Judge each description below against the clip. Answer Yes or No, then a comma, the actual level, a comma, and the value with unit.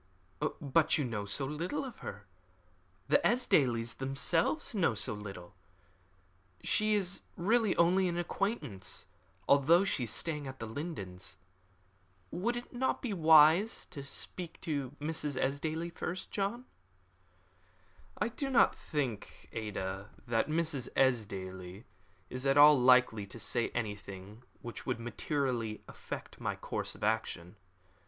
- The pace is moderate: No, slow, 130 wpm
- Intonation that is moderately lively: No, wide, 7.5 semitones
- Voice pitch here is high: No, medium, 140 Hz